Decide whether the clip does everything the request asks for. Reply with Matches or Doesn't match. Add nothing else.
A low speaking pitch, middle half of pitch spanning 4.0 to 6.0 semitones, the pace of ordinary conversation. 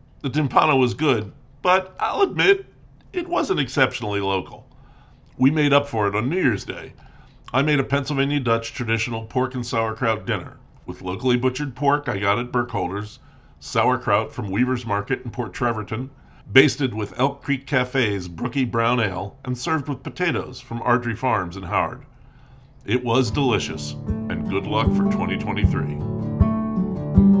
Doesn't match